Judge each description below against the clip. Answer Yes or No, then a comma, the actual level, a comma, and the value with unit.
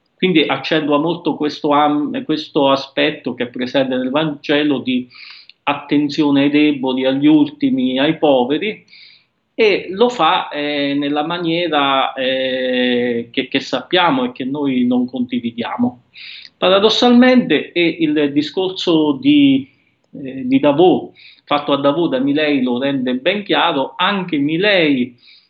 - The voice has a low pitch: No, medium, 150 Hz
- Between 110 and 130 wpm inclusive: Yes, average, 125 wpm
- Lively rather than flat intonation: Yes, wide, 6.2 semitones